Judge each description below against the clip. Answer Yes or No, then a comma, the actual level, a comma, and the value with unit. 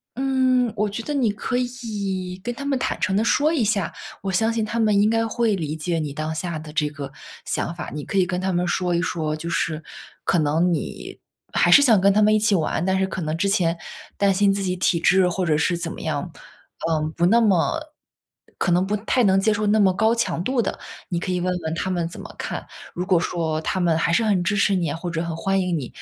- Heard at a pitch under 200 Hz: Yes, high, 190 Hz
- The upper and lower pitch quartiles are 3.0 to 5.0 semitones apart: Yes, average, 4.1 semitones